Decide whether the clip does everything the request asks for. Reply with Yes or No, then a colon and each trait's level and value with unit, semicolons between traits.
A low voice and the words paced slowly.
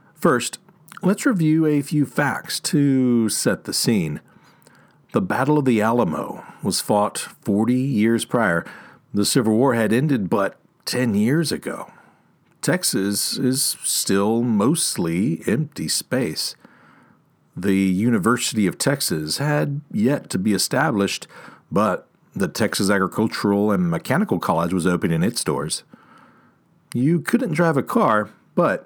Yes: low, 120 Hz; slow, 130 wpm